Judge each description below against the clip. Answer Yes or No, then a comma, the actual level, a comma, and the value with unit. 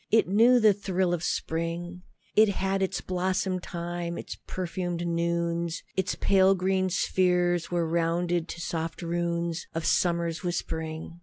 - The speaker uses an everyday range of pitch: No, narrow, 1.8 semitones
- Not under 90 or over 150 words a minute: Yes, average, 140 wpm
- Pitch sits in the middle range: Yes, medium, 175 Hz